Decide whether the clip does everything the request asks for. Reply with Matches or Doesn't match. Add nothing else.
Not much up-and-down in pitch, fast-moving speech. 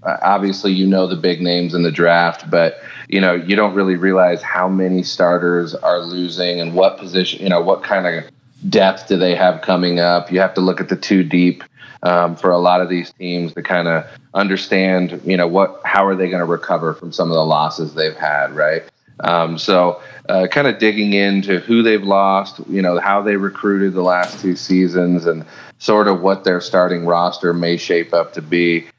Matches